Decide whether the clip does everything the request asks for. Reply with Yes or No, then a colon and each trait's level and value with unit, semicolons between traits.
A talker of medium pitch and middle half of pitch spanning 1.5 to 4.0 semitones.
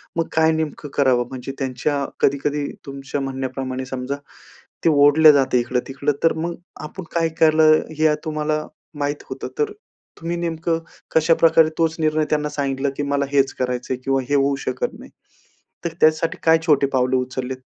Yes: medium, 145 Hz; average, 2.9 semitones